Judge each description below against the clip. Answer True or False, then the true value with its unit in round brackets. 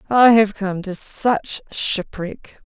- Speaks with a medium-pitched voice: False (205 Hz)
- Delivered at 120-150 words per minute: True (135 wpm)